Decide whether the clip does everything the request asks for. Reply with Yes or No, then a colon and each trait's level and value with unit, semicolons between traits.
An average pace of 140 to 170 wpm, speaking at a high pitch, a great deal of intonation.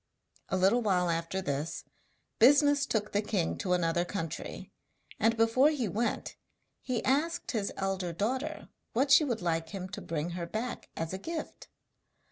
Yes: average, 160 wpm; high, 205 Hz; wide, 6.0 semitones